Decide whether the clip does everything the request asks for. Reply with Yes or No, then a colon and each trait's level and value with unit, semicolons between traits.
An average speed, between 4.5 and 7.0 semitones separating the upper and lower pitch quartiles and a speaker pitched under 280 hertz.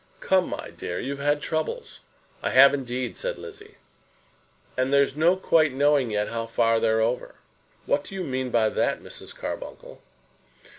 Yes: average, 160 wpm; average, 4.9 semitones; medium, 140 Hz